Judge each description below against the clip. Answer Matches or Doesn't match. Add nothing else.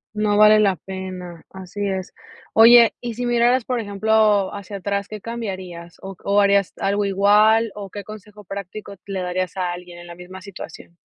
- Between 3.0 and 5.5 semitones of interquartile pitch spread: Doesn't match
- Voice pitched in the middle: Doesn't match